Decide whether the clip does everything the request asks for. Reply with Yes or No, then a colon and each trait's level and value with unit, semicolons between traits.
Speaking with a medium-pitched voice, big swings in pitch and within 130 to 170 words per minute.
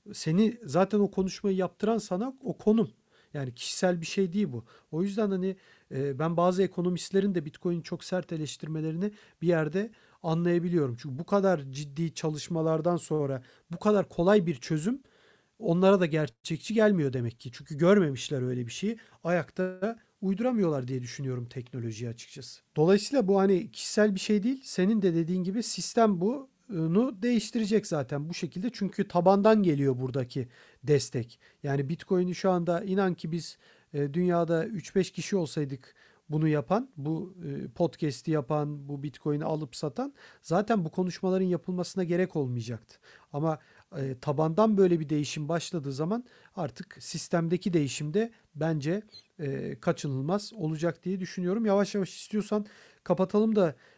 No: medium, 175 Hz; average, 4.6 semitones; fast, 140 wpm